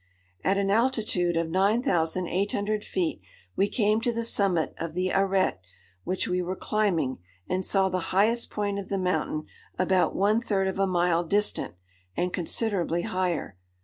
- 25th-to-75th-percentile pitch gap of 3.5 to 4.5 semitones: No, average, 2.7 semitones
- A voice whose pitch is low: No, high, 190 Hz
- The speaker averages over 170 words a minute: No, average, 155 wpm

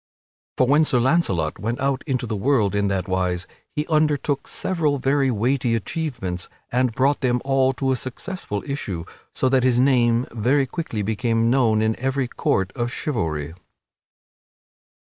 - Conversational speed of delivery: Yes, average, 155 wpm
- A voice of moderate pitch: No, low, 125 Hz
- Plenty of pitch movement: No, average, 4.2 semitones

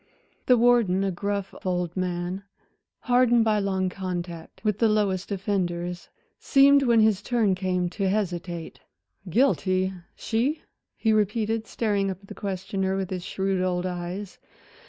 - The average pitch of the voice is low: No, high, 195 Hz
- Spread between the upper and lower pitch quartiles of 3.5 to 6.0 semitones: No, average, 3.0 semitones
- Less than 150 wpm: Yes, average, 140 wpm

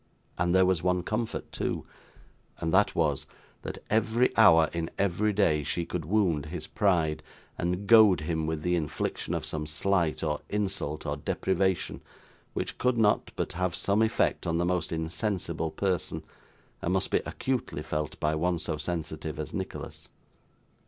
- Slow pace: No, average, 160 wpm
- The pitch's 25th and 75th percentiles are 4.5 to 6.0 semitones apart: No, average, 3.9 semitones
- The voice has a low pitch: Yes, very low, 85 Hz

